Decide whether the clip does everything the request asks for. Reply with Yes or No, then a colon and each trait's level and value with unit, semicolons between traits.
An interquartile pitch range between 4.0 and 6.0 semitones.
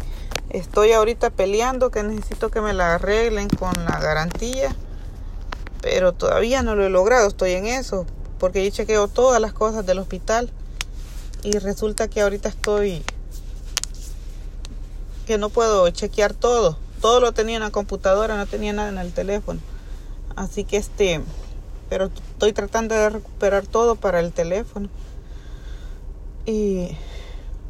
No: average, 3.3 semitones